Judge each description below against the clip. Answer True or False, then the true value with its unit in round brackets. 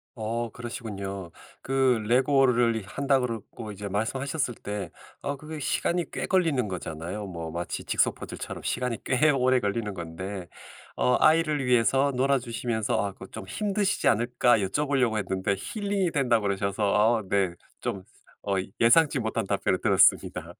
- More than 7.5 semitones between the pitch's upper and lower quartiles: False (5.1 semitones)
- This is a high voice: False (115 Hz)